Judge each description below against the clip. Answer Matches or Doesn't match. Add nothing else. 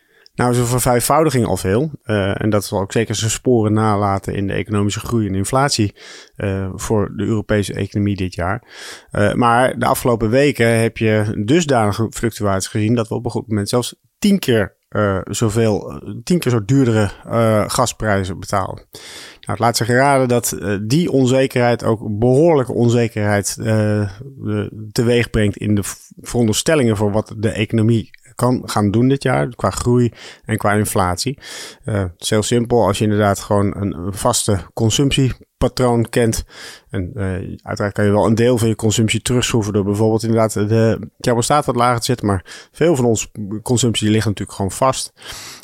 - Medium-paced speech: Matches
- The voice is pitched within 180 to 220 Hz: Doesn't match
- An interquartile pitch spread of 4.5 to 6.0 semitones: Doesn't match